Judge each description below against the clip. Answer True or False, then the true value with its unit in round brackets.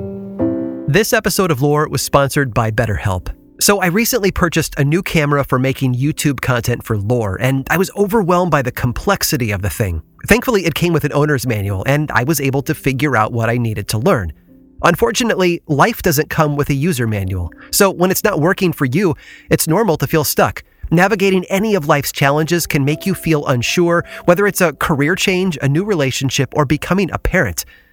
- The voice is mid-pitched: True (150 Hz)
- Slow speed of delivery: False (200 wpm)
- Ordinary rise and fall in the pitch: False (6.3 semitones)